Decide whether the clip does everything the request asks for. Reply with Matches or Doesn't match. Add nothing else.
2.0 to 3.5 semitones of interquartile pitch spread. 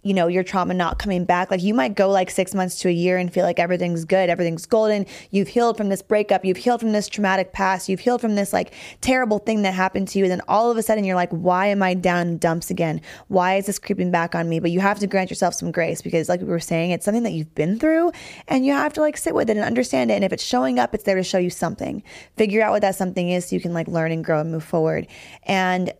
Matches